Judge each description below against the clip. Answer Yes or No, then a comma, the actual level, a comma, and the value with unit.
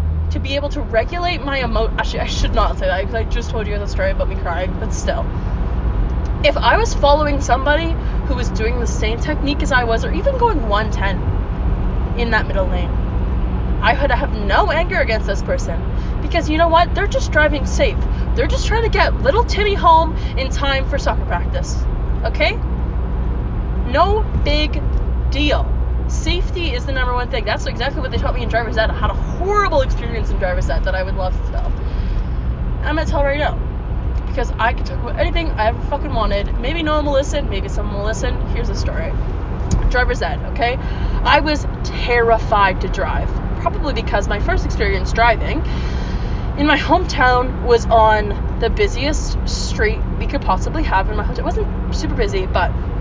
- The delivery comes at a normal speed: Yes, average, 190 wpm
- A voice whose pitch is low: Yes, very low, 80 Hz